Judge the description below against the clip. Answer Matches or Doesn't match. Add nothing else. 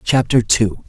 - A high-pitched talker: Doesn't match